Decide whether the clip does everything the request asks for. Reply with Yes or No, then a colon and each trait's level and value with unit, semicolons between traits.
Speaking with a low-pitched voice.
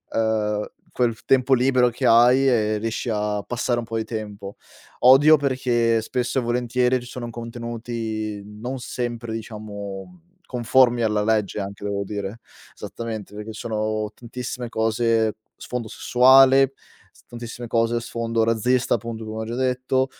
Yes: low, 115 Hz